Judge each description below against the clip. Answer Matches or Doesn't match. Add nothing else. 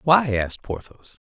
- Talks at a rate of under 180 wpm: Matches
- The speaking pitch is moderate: Doesn't match